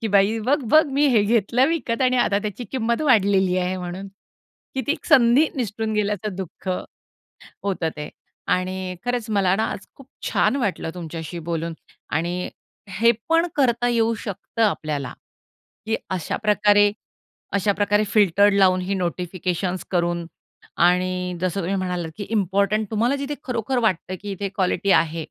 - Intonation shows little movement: No, average, 4.0 semitones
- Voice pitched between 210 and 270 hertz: No, high, 200 Hz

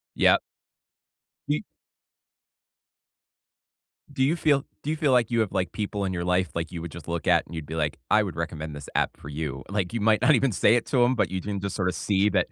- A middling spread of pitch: No, wide, 5.8 semitones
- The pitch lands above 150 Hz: No, very low, 95 Hz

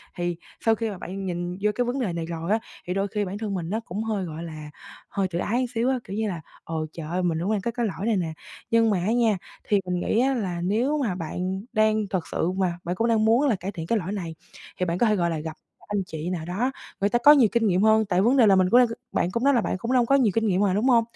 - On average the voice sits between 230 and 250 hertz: No, high, 200 Hz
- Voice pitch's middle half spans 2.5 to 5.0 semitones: Yes, average, 4.2 semitones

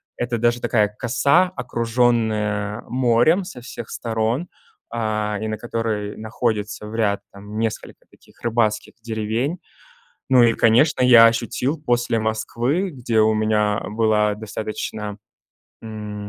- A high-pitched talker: No, low, 115 Hz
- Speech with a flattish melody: Yes, narrow, 2.2 semitones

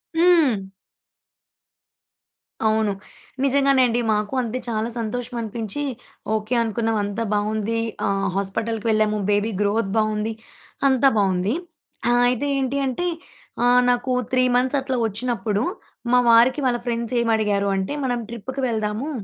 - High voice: Yes, high, 230 Hz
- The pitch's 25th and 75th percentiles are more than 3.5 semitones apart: No, average, 2.9 semitones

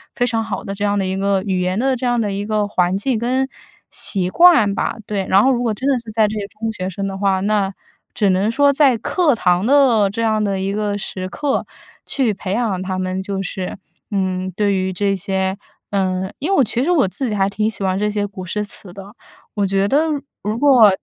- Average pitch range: Yes, average, 3.2 semitones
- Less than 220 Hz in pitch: Yes, high, 205 Hz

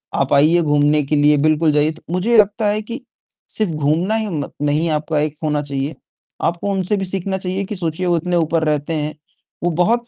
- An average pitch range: Yes, average, 4.2 semitones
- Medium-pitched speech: Yes, medium, 165 Hz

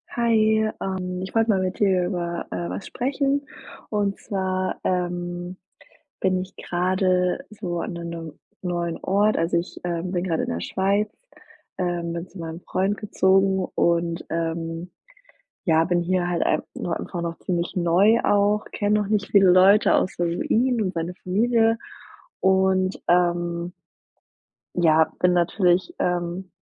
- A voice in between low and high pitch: Yes, medium, 180 Hz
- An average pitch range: No, narrow, 2.3 semitones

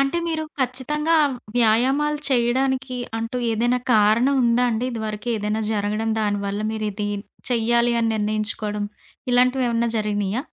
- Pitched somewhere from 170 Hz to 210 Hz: No, high, 230 Hz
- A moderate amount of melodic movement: Yes, average, 3.0 semitones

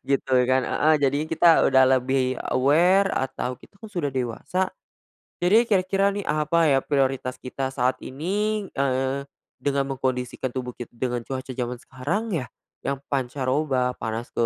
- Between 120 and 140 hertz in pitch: Yes, low, 135 Hz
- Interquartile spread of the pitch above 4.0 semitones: Yes, average, 4.5 semitones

